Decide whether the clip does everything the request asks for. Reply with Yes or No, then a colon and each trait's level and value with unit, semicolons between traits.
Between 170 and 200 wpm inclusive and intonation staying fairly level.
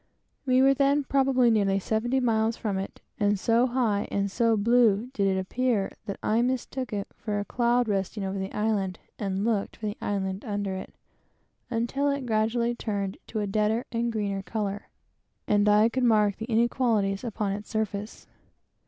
No: average, 175 wpm; average, 3.0 semitones